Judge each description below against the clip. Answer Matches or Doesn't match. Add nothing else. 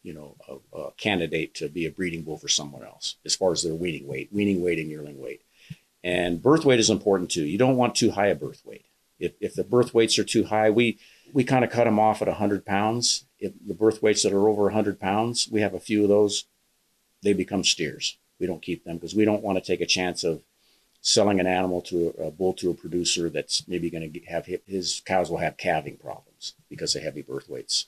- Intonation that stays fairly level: Doesn't match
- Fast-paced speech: Matches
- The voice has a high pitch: Doesn't match